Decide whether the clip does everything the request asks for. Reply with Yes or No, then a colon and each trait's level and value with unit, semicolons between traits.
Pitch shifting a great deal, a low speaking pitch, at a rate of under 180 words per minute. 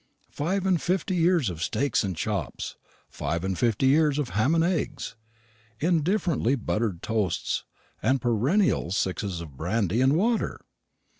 Yes: wide, 8.8 semitones; low, 130 Hz; average, 140 wpm